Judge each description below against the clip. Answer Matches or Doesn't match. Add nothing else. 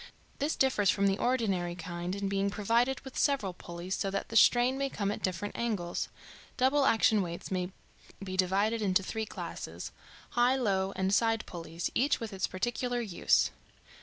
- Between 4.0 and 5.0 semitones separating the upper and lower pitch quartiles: Matches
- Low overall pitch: Doesn't match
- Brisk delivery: Doesn't match